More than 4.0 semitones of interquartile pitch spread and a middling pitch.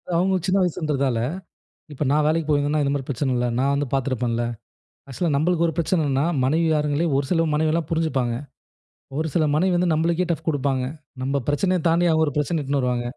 No: average, 3.2 semitones; medium, 150 Hz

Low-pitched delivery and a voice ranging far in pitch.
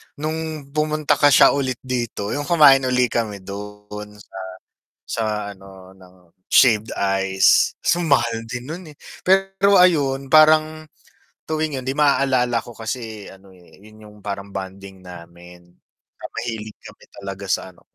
Yes: low, 120 Hz; wide, 6.7 semitones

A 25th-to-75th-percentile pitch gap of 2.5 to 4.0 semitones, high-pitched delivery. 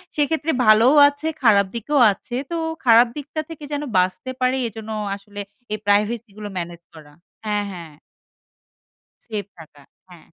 No: average, 4.7 semitones; high, 215 Hz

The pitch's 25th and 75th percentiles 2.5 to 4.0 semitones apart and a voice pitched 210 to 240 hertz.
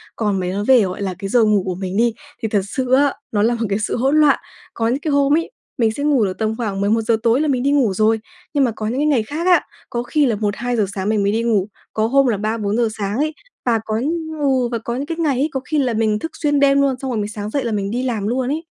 No: average, 4.4 semitones; high, 235 Hz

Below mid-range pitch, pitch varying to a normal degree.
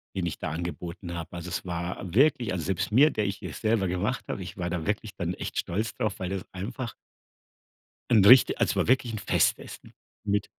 Yes: very low, 95 Hz; average, 3.9 semitones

